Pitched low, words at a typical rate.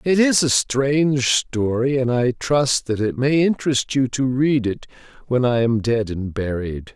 Yes: low, 125 Hz; average, 190 wpm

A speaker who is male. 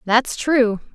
No: female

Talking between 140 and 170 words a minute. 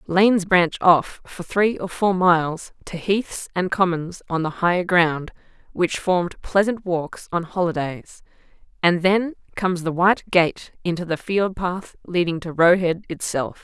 Yes: average, 165 wpm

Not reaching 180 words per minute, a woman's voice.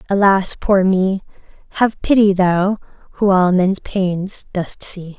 Yes: average, 140 wpm; female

